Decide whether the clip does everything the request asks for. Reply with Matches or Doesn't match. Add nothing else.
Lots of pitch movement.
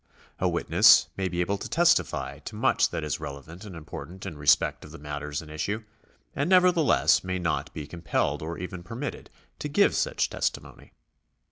Matches